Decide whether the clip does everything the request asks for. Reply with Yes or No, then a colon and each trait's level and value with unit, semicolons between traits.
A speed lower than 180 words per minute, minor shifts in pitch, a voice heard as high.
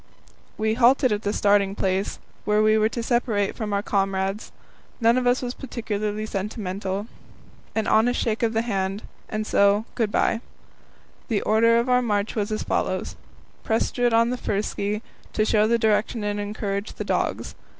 Yes: average, 170 wpm; narrow, 2.2 semitones; high, 215 Hz